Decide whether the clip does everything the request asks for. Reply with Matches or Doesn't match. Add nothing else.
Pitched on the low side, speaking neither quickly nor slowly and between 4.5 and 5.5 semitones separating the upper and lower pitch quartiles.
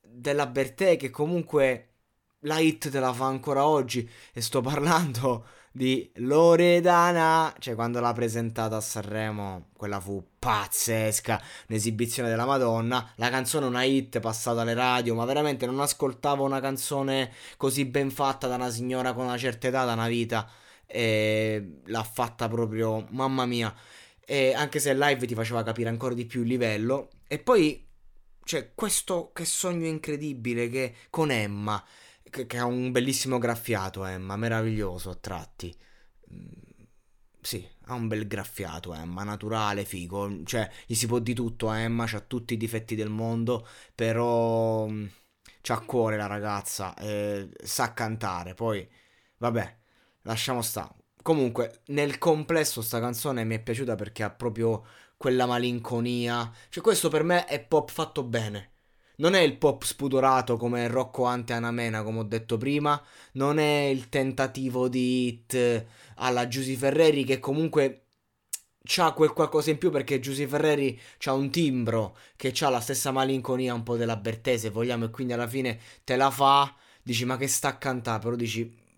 Doesn't match